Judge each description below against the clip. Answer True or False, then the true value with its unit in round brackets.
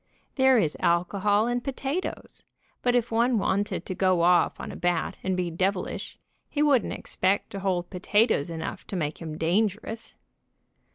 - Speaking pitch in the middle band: False (195 Hz)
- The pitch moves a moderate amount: True (4.6 semitones)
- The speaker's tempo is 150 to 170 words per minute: True (160 wpm)